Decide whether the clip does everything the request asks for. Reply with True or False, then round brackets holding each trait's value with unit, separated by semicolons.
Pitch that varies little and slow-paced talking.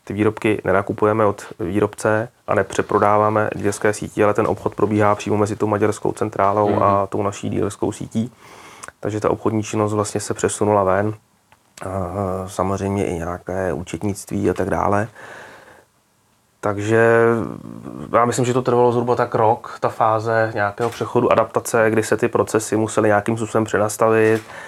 False (1.8 semitones; 145 wpm)